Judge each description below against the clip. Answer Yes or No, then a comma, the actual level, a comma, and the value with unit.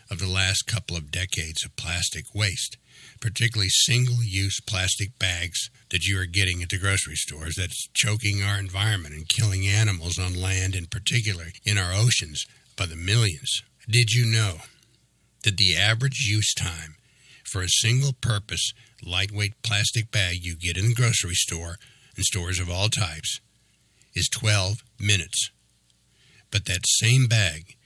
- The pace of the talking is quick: No, average, 155 wpm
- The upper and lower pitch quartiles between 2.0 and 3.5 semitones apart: No, average, 4.1 semitones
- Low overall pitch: Yes, low, 105 Hz